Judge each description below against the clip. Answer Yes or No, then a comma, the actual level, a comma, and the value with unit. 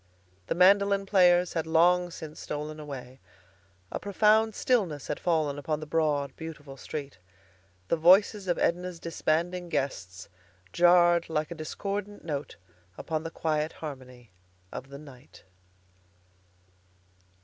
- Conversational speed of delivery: No, slow, 125 wpm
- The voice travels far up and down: No, average, 3.3 semitones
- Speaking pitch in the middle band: Yes, medium, 160 Hz